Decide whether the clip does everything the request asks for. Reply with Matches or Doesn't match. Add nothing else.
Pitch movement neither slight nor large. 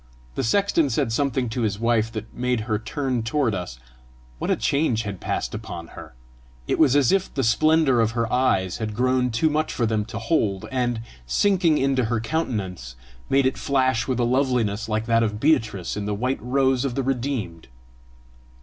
Matches